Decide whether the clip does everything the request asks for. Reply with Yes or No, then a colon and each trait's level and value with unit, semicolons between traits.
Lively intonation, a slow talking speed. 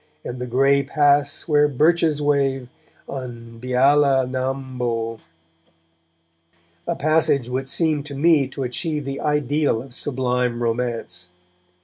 No: average, 2.8 semitones; slow, 120 wpm